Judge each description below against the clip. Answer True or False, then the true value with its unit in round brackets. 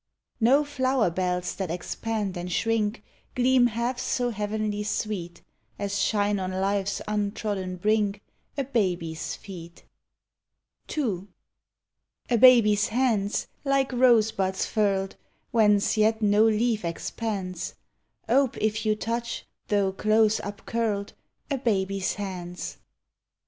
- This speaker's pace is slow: True (110 wpm)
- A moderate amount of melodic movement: True (3.0 semitones)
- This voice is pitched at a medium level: False (210 Hz)